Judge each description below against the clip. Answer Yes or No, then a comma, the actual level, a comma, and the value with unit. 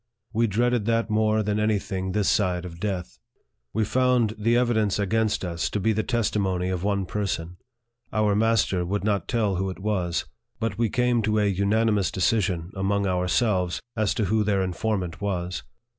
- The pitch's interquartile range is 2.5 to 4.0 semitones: Yes, average, 2.9 semitones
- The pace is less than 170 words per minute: No, average, 175 wpm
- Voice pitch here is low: Yes, low, 105 Hz